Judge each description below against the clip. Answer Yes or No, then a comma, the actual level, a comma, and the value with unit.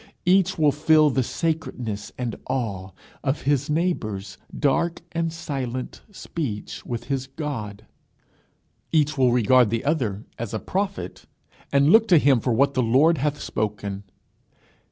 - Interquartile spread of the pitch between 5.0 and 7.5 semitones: Yes, wide, 5.4 semitones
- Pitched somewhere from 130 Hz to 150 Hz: Yes, low, 135 Hz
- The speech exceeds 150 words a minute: No, average, 140 wpm